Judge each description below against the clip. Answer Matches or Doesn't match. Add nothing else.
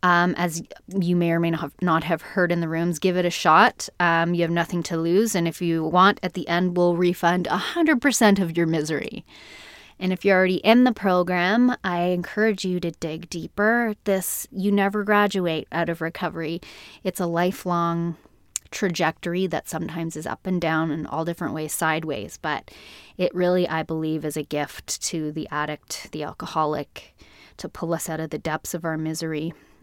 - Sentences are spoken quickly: Doesn't match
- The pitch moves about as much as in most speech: Doesn't match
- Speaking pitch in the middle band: Matches